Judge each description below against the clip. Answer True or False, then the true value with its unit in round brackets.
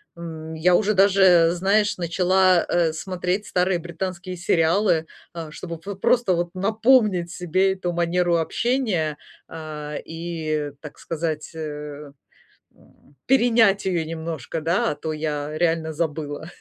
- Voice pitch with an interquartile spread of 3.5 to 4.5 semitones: False (3.0 semitones)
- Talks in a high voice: False (170 Hz)